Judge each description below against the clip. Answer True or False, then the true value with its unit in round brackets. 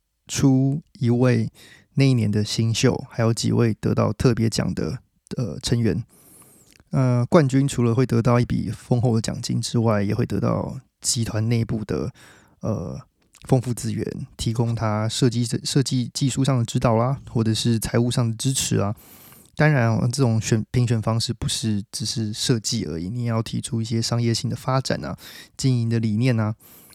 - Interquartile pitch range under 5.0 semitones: True (2.4 semitones)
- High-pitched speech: False (120 Hz)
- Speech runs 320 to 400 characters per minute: False (255 characters per minute)